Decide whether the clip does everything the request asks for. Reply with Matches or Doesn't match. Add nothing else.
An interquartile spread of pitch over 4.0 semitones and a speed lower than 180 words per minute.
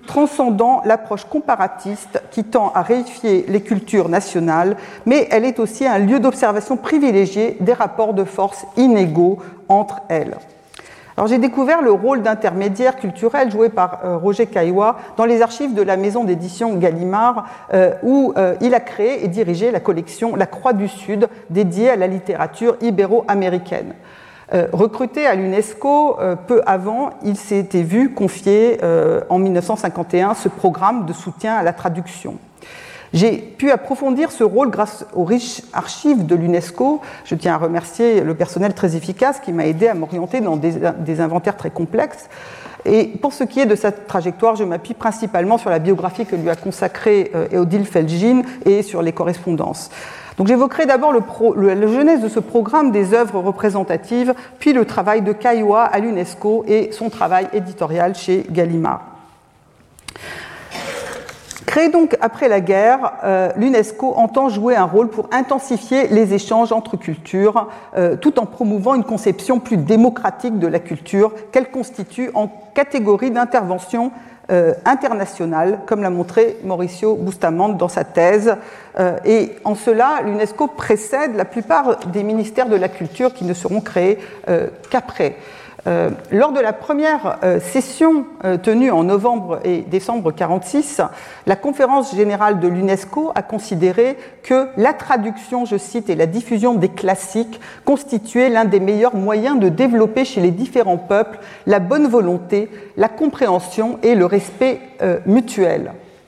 Matches